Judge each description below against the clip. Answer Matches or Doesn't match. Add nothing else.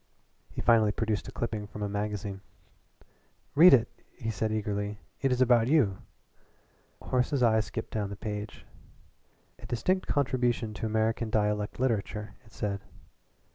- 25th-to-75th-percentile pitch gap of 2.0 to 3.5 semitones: Matches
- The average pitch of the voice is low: Matches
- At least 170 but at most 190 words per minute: Doesn't match